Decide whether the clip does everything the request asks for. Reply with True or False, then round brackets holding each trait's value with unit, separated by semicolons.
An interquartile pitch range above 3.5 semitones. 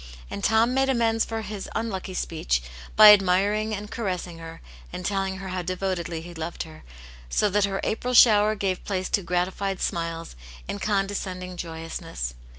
False (3.1 semitones)